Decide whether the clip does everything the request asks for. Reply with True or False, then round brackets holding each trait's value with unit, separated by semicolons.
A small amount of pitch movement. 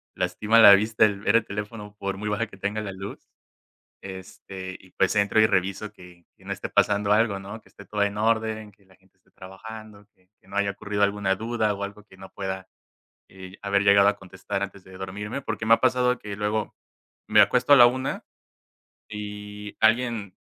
True (1.9 semitones)